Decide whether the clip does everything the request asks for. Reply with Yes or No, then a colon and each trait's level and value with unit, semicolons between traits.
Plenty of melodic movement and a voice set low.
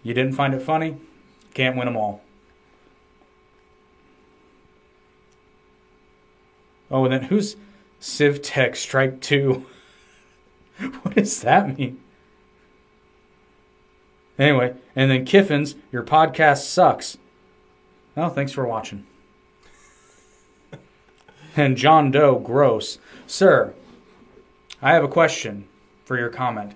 Yes: wide, 7.3 semitones; low, 130 Hz